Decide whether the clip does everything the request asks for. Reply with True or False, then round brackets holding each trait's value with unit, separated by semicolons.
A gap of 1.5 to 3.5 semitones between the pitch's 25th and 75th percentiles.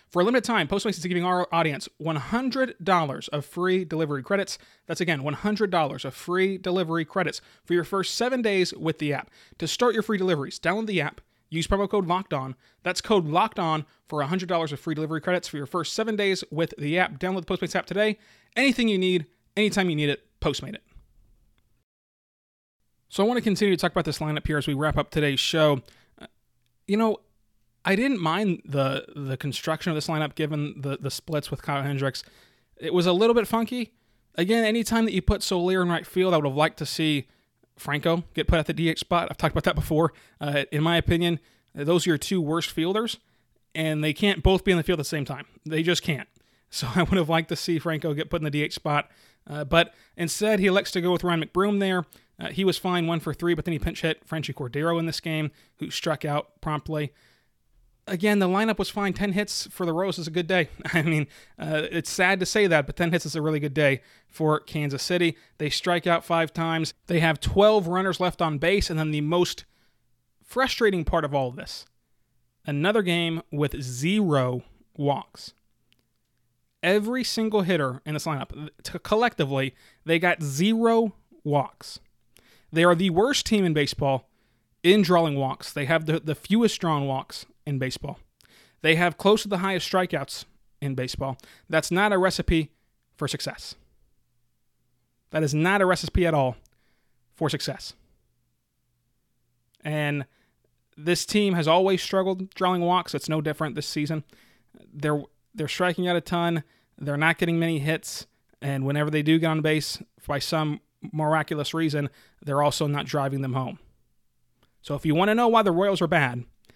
False (4.0 semitones)